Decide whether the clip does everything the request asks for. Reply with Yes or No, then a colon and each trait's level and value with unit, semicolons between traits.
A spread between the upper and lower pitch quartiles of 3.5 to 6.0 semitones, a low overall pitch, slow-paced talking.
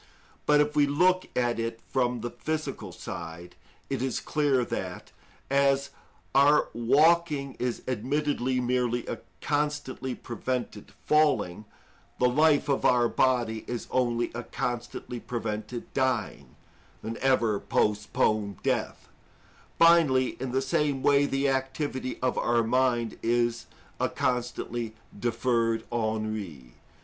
No: average, 3.1 semitones; low, 125 Hz; slow, 120 wpm